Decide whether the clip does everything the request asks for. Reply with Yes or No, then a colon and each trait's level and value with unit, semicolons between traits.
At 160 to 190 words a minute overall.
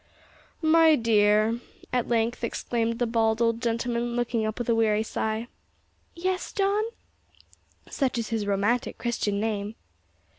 No: slow, 135 wpm